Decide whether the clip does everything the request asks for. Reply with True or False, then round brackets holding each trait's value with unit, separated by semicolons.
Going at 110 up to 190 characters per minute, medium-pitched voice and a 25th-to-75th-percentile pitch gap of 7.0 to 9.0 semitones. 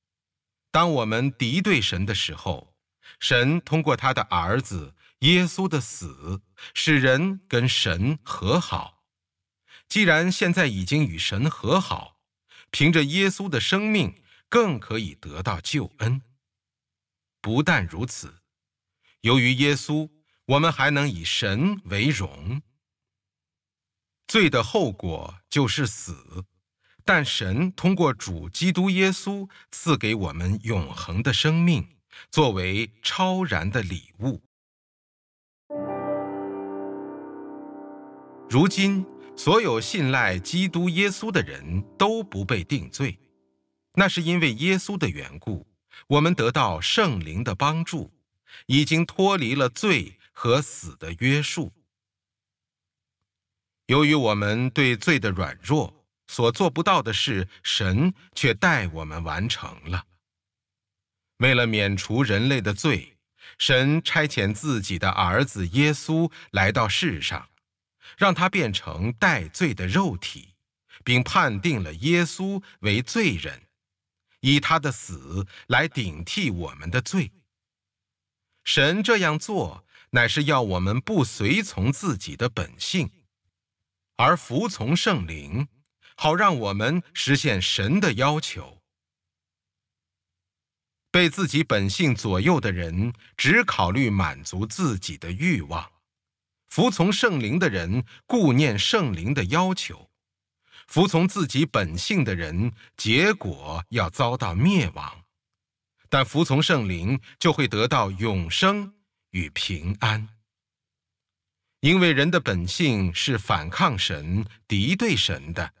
False (170 characters per minute; 115 Hz; 8.6 semitones)